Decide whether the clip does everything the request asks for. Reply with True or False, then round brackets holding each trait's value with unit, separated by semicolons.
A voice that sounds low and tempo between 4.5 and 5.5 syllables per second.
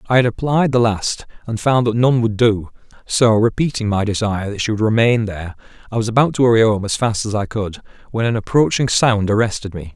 False (110 Hz; 5.8 syllables/s)